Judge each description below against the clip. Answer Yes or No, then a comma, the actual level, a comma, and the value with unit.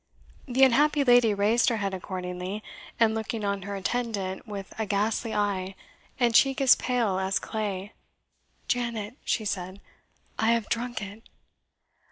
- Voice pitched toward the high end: Yes, high, 215 Hz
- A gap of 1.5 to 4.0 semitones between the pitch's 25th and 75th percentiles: Yes, average, 3.3 semitones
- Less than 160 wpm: Yes, average, 145 wpm